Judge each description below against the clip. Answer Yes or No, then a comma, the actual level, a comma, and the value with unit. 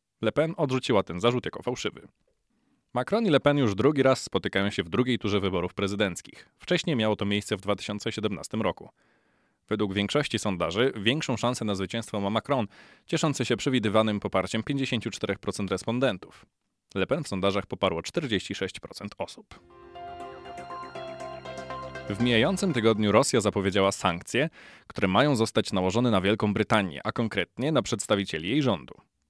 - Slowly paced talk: No, average, 140 wpm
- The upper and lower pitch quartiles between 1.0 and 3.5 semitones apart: No, average, 4.7 semitones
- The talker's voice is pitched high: No, low, 110 Hz